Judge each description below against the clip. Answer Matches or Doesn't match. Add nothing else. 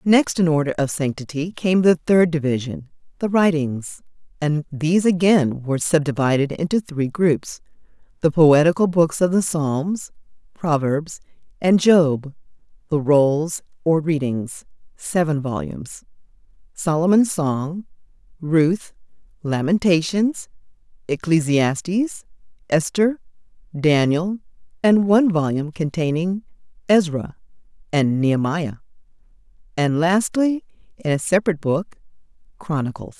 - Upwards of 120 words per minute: Doesn't match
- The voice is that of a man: Doesn't match